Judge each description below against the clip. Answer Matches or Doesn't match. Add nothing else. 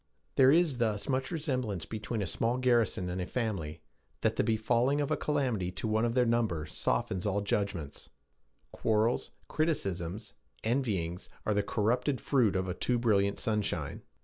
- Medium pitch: Doesn't match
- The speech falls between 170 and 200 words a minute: Doesn't match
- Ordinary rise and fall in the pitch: Matches